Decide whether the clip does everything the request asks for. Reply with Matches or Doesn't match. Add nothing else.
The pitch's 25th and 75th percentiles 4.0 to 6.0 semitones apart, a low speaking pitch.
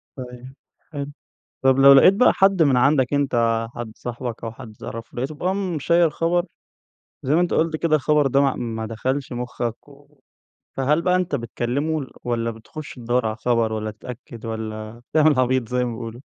Matches